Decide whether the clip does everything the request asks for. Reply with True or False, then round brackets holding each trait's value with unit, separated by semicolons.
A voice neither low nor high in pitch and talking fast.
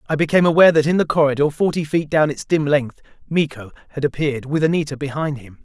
True (150 Hz; 215 wpm)